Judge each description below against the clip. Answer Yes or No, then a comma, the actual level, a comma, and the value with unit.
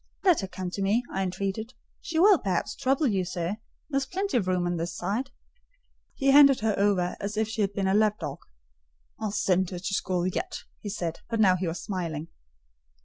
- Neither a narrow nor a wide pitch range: Yes, average, 3.7 semitones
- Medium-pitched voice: No, high, 200 Hz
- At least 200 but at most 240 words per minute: Yes, fast, 205 wpm